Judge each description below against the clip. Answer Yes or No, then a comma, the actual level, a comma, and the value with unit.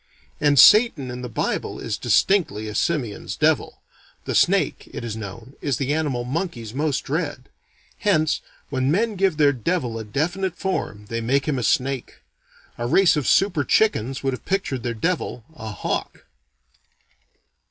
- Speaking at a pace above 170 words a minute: No, average, 165 wpm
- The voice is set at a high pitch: No, low, 135 Hz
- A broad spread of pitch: Yes, wide, 6.2 semitones